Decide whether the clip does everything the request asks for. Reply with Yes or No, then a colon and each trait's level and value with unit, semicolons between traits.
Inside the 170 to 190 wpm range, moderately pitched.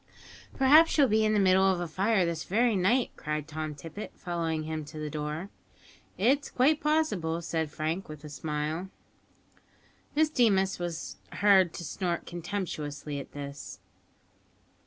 No: average, 155 wpm; medium, 175 Hz